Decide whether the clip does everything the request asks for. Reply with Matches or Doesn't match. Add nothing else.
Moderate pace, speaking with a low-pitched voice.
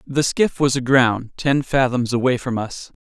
Matches